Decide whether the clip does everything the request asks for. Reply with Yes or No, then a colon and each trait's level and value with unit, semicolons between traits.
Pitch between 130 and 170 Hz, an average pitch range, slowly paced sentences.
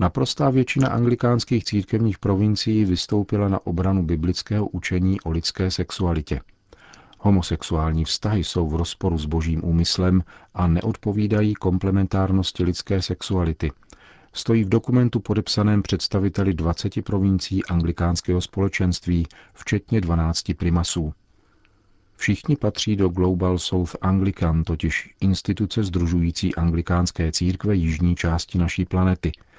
No: very low, 95 Hz; average, 3.2 semitones; slow, 105 wpm